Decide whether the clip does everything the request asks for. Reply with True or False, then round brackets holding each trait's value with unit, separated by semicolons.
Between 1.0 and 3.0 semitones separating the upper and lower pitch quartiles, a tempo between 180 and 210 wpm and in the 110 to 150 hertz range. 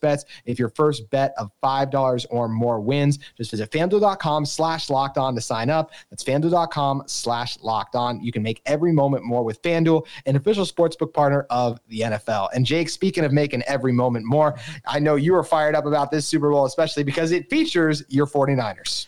False (4.4 semitones; 200 wpm; 140 Hz)